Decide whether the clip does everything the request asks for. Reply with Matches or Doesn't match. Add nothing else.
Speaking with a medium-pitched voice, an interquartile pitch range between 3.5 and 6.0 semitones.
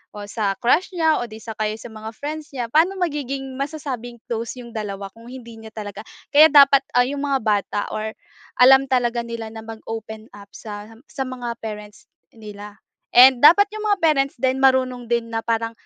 Doesn't match